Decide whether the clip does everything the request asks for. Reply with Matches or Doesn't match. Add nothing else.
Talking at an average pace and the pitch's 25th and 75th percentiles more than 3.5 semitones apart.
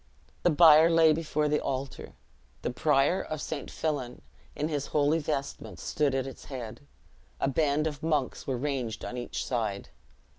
Doesn't match